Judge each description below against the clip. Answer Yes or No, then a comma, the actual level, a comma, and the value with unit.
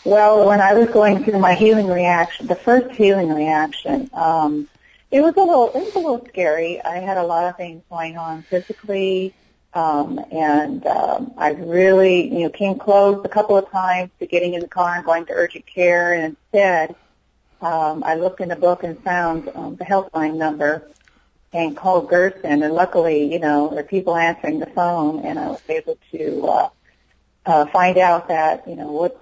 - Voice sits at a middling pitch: Yes, medium, 175 Hz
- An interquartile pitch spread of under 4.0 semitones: Yes, average, 3.4 semitones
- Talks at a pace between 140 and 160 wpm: No, average, 190 wpm